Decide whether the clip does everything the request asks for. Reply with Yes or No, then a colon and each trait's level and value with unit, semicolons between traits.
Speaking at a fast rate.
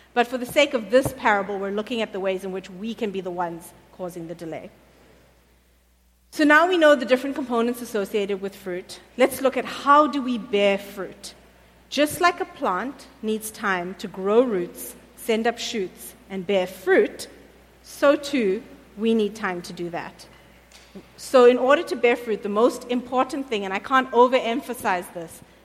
No: average, 185 wpm